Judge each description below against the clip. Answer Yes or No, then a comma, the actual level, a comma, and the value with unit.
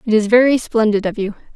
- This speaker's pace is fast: Yes, fast, 230 wpm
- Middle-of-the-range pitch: No, high, 220 Hz